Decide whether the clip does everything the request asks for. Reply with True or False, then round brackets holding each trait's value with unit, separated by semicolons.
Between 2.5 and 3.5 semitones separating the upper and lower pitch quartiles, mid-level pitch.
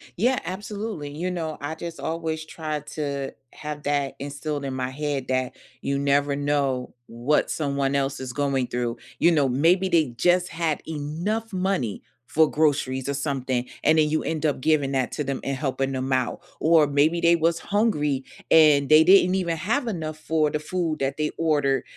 True (3.1 semitones; 150 Hz)